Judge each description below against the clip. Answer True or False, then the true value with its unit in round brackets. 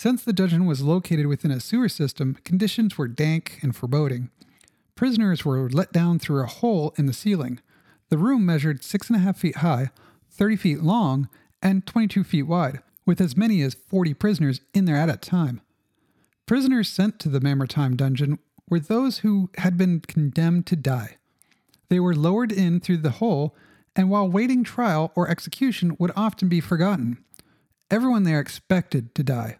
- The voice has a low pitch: False (170 Hz)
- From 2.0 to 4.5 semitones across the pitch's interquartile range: False (5.6 semitones)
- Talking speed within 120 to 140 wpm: False (175 wpm)